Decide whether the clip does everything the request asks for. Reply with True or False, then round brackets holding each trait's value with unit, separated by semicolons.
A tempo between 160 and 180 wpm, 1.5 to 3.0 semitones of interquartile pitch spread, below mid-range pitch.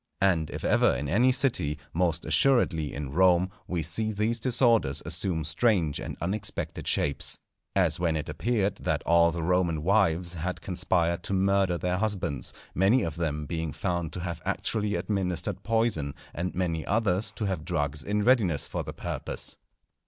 False (165 wpm; 4.0 semitones; 90 Hz)